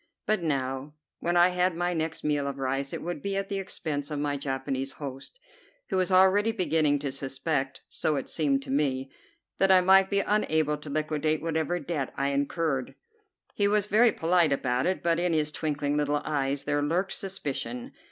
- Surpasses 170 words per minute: Yes, average, 190 wpm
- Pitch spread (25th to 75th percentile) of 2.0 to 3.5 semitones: No, average, 4.3 semitones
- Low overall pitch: No, medium, 155 Hz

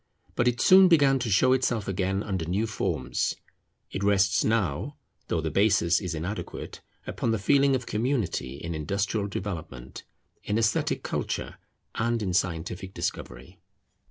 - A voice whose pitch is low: Yes, low, 100 Hz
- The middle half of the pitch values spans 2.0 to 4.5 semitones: No, average, 5.2 semitones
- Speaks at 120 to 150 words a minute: Yes, average, 145 wpm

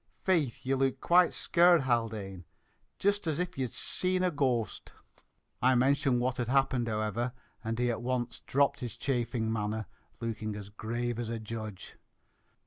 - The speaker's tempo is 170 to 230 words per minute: No, average, 160 wpm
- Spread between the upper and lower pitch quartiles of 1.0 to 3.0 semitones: No, average, 3.4 semitones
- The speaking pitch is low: Yes, low, 120 Hz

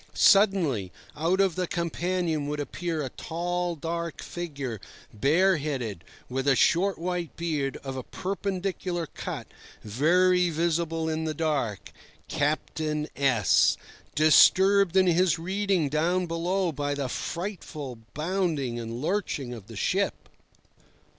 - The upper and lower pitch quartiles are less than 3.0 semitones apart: No, average, 4.2 semitones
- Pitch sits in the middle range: Yes, medium, 165 Hz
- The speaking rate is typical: No, slow, 120 wpm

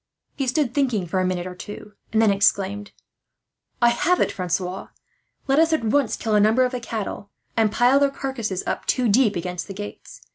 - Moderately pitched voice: No, high, 220 Hz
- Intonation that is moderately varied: Yes, average, 4.7 semitones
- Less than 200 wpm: No, fast, 205 wpm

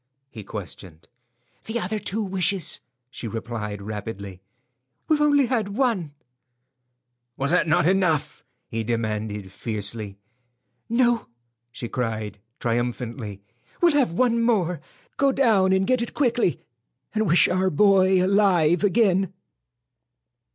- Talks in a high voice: No, medium, 175 Hz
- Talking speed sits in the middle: No, slow, 115 wpm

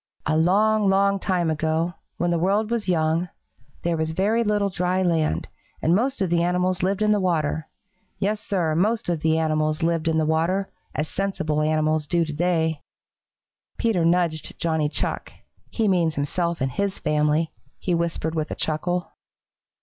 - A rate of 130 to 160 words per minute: No, average, 170 wpm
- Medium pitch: Yes, medium, 170 Hz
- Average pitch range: Yes, average, 3.3 semitones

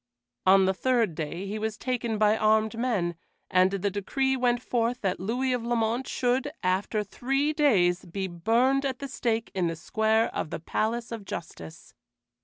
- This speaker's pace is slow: No, average, 175 wpm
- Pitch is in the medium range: No, high, 220 Hz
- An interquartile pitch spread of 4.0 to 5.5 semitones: Yes, average, 4.5 semitones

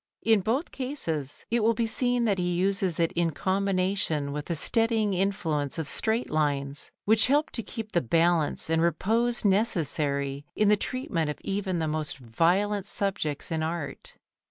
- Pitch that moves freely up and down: Yes, wide, 5.7 semitones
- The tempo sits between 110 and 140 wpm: No, average, 165 wpm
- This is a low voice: No, medium, 185 Hz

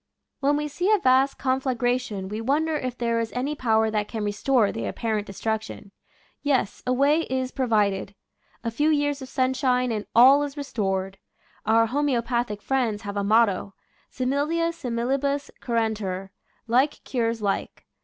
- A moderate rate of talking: Yes, average, 165 wpm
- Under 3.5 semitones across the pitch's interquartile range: No, average, 3.9 semitones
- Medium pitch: No, high, 245 Hz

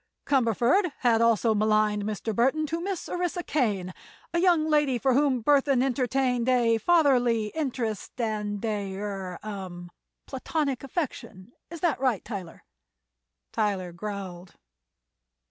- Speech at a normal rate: No, slow, 115 wpm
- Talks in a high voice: Yes, high, 235 Hz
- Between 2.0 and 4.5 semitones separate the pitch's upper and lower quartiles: No, average, 5.2 semitones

